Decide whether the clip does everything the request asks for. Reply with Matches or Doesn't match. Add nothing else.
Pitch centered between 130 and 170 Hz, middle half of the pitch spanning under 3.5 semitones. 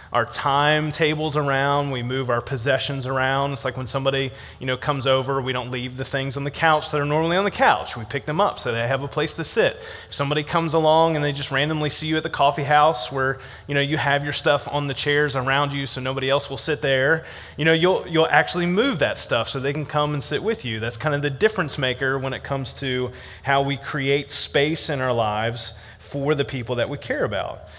Matches